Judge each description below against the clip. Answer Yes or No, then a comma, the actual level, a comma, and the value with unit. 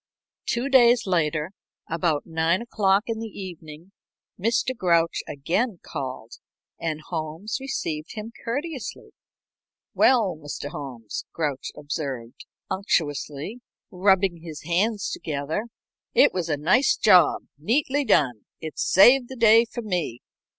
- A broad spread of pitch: Yes, wide, 6.8 semitones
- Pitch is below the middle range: No, medium, 180 Hz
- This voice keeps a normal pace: No, slow, 120 wpm